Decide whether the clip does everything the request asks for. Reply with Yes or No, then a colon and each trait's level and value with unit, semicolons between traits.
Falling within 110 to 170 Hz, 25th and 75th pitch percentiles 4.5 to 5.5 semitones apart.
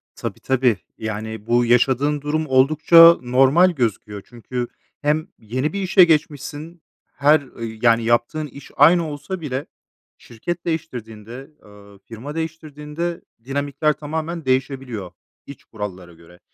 Yes: low, 135 Hz; average, 5.0 semitones